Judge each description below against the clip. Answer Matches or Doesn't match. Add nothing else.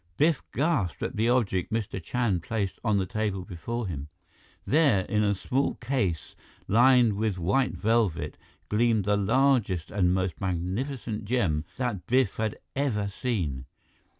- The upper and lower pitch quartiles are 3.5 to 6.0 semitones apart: Matches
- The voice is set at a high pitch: Doesn't match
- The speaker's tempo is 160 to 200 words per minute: Doesn't match